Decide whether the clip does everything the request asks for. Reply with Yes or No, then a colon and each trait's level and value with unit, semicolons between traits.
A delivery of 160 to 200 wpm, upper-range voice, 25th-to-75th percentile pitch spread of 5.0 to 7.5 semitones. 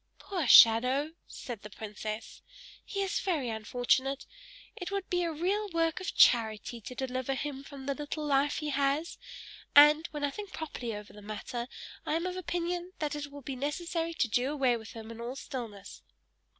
Yes: average, 185 wpm; very high, 280 Hz; wide, 5.4 semitones